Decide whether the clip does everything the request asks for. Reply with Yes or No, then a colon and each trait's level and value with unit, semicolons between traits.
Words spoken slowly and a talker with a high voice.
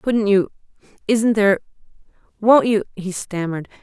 Yes: slow, 95 wpm; high, 205 Hz